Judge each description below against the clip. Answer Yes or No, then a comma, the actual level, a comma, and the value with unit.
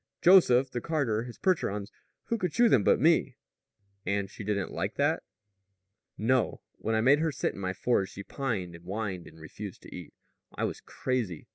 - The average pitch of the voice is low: Yes, low, 110 Hz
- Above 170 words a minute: Yes, average, 185 wpm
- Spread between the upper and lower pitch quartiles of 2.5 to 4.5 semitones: No, wide, 5.5 semitones